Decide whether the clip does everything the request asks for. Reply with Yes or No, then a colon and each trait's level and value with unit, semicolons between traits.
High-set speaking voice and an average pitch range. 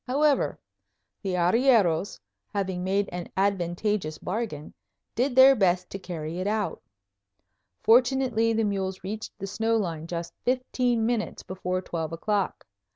Yes: high, 200 Hz; average, 4.2 semitones